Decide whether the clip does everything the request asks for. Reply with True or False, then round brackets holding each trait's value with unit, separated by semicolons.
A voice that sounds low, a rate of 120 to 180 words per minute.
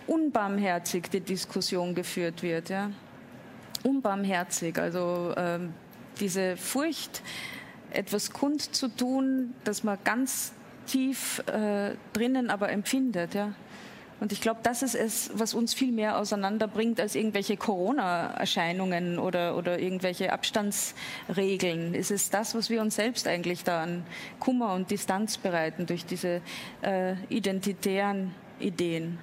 False (200 Hz; 125 wpm)